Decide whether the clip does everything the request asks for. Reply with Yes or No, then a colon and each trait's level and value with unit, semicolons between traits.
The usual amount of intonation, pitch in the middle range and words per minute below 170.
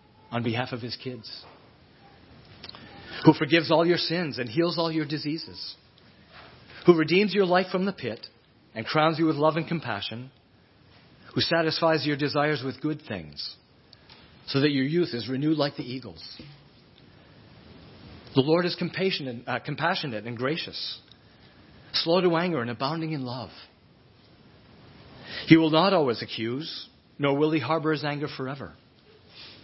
Yes: average, 4.9 semitones; medium, 150 Hz; average, 145 wpm